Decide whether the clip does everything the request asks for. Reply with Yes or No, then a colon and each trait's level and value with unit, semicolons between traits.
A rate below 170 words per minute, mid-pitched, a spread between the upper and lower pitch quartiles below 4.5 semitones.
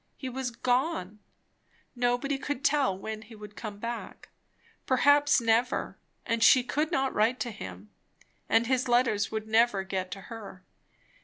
No: average, 150 wpm; high, 235 Hz; average, 3.6 semitones